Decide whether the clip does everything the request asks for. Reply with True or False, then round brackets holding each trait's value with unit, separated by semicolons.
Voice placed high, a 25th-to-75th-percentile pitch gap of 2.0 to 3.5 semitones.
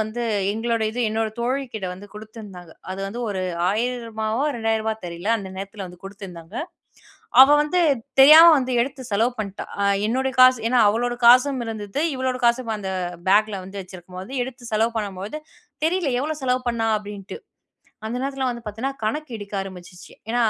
False (225 Hz; 4.1 semitones)